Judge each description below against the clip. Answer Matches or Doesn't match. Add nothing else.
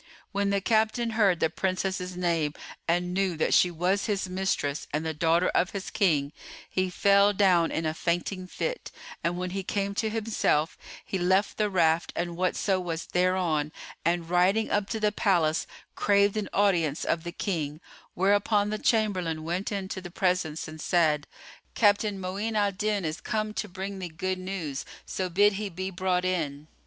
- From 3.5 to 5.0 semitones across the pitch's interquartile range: Doesn't match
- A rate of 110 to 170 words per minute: Doesn't match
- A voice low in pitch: Doesn't match